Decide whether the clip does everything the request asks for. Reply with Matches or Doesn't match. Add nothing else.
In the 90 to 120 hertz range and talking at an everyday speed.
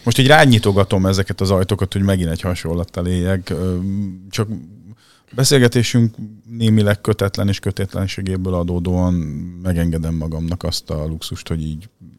Matches